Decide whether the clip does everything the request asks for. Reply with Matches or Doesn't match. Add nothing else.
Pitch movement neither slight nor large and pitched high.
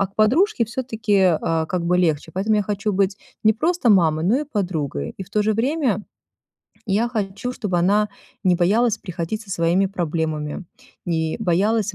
Matches